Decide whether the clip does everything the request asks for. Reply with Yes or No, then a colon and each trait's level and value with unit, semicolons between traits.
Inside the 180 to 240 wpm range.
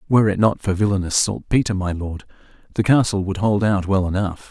Yes: average, 200 wpm